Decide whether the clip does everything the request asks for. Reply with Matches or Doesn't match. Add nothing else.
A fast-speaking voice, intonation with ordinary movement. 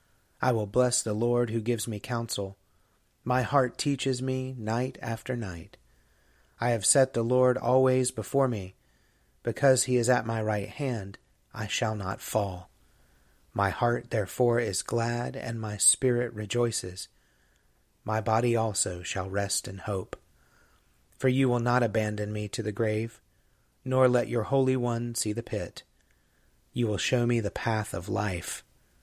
Doesn't match